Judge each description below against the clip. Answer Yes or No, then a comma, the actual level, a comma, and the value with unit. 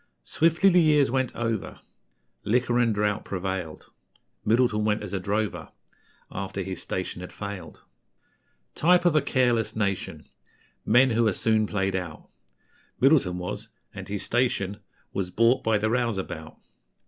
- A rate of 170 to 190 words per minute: No, average, 140 wpm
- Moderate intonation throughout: Yes, average, 4.1 semitones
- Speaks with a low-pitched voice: Yes, low, 110 Hz